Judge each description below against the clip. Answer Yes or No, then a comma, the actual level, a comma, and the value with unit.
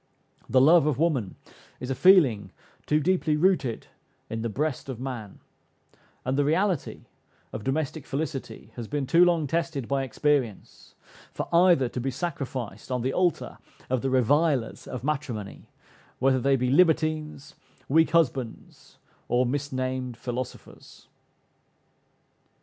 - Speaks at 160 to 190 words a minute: No, slow, 135 wpm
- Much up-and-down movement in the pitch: No, average, 3.7 semitones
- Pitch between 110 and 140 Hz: Yes, low, 135 Hz